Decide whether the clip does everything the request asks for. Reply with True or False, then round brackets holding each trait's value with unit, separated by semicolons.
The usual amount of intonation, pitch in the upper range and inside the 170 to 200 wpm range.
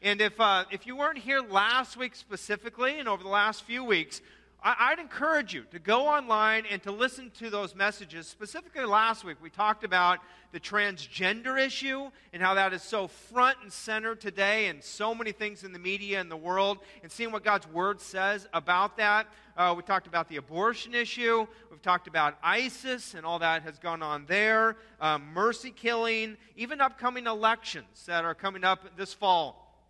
True (3.9 semitones; 205 Hz; 190 wpm)